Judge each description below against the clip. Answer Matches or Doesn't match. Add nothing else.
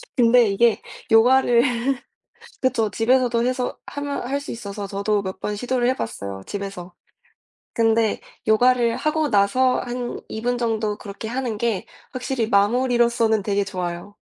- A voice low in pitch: Doesn't match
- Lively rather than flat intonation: Doesn't match